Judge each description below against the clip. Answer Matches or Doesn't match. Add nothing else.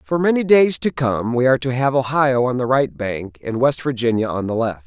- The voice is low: Matches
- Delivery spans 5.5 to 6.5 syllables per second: Doesn't match